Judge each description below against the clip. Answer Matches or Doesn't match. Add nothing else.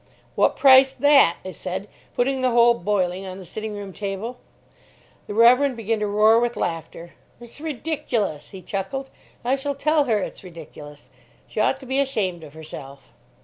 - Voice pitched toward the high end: Matches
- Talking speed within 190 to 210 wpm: Doesn't match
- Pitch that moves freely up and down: Matches